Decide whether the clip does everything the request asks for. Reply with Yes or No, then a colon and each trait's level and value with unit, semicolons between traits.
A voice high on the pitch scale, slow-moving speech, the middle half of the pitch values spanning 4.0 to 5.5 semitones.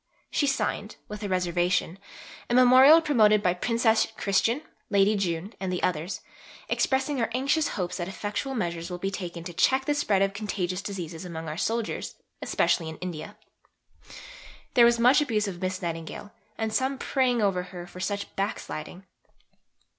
No: high, 200 Hz; average, 160 wpm; average, 4.8 semitones